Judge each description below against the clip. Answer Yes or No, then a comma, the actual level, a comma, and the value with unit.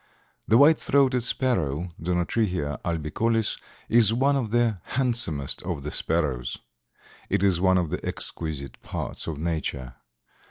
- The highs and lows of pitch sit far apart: Yes, wide, 7.4 semitones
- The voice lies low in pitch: Yes, very low, 90 Hz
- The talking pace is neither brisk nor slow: No, slow, 130 wpm